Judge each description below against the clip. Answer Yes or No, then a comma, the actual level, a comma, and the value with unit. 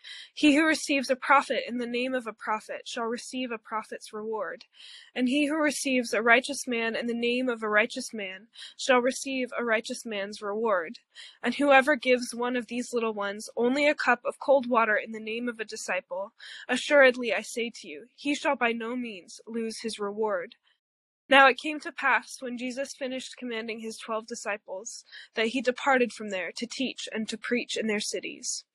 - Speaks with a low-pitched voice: No, high, 240 Hz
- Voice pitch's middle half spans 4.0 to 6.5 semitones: No, average, 3.1 semitones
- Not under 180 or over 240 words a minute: Yes, average, 195 wpm